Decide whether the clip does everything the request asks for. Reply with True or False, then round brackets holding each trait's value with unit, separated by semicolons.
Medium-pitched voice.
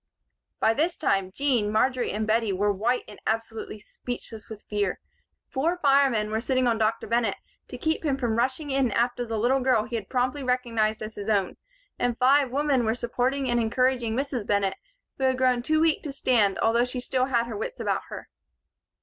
False (245 Hz)